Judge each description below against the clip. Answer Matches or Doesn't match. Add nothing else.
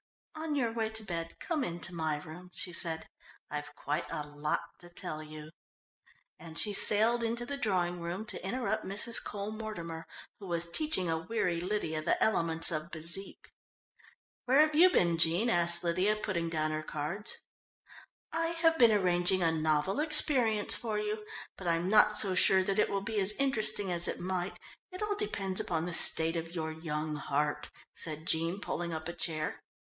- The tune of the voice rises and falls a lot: Doesn't match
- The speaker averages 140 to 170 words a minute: Doesn't match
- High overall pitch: Doesn't match